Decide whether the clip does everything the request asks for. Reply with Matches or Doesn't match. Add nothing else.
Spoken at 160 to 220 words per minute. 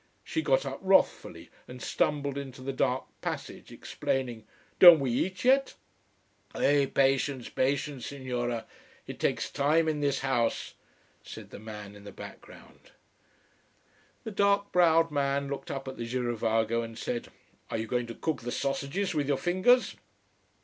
Doesn't match